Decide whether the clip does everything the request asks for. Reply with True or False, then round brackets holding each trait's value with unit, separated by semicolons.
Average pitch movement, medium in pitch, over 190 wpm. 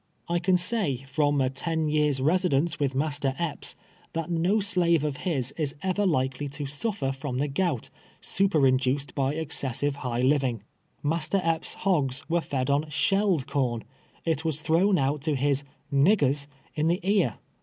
False (3.9 semitones; 150 Hz; 165 wpm)